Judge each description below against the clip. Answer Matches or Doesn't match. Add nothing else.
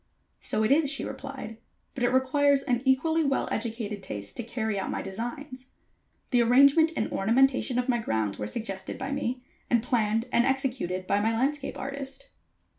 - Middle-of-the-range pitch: Doesn't match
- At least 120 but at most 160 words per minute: Doesn't match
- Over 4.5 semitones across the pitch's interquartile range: Doesn't match